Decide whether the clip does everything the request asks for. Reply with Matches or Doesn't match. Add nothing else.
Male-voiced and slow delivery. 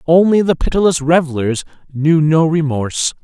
Matches